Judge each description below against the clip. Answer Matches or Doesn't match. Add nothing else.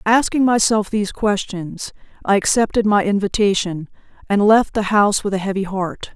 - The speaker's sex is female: Matches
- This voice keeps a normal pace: Matches